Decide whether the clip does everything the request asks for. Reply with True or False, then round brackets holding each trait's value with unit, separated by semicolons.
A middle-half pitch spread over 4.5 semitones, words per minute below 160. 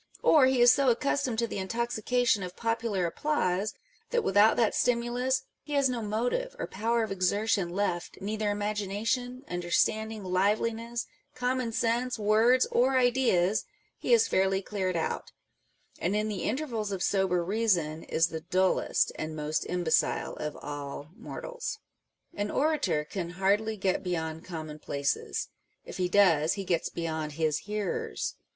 True (5.0 semitones; 150 wpm)